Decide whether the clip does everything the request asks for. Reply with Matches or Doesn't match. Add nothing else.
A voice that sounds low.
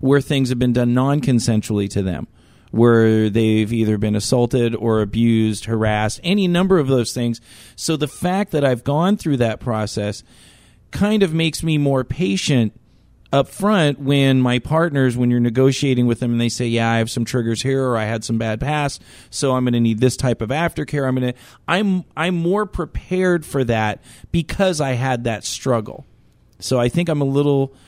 Matches